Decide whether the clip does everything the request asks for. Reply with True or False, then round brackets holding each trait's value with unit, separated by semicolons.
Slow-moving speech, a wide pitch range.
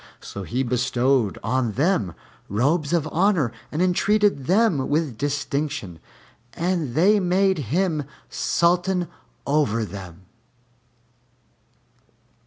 True (95 wpm; 6.6 semitones)